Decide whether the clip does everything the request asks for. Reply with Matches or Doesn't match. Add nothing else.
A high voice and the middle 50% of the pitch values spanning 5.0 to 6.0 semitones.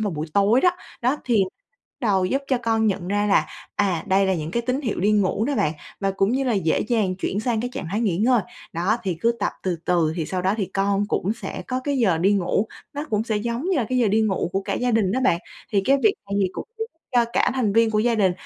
Doesn't match